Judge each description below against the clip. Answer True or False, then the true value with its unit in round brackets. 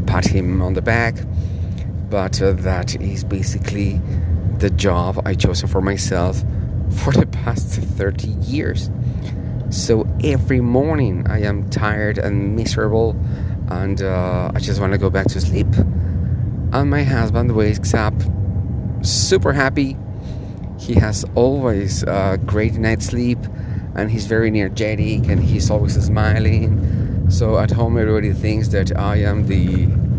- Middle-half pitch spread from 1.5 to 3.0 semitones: True (2.5 semitones)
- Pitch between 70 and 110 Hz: True (105 Hz)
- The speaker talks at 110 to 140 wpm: True (135 wpm)